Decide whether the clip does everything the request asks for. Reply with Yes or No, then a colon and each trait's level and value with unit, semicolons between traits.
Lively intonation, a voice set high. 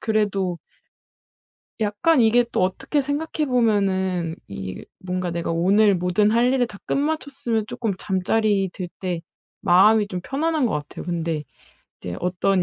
No: average, 4.5 semitones; high, 200 Hz